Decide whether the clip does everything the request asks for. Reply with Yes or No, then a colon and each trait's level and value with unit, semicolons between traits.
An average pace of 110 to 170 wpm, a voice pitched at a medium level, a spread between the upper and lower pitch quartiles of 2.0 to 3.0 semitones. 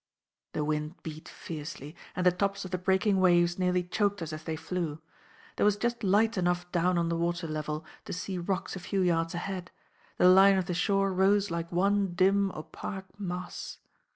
No: average, 190 wpm; medium, 180 Hz; narrow, 2.5 semitones